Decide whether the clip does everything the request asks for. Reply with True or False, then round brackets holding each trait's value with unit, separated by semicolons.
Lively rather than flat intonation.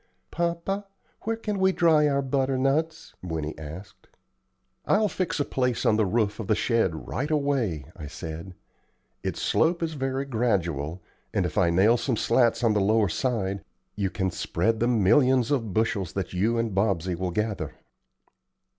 True (6.7 semitones)